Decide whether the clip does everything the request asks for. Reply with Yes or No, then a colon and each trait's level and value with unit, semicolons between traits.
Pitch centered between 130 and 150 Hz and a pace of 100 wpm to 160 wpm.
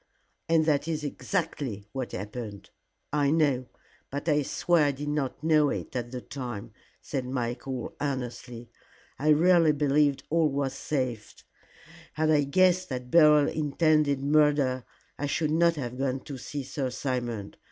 Yes: medium, 140 Hz; average, 150 wpm